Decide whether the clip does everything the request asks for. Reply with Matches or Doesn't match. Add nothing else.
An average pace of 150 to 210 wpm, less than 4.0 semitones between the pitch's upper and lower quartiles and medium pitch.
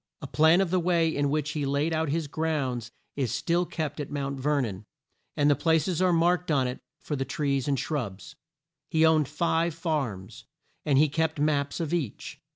Matches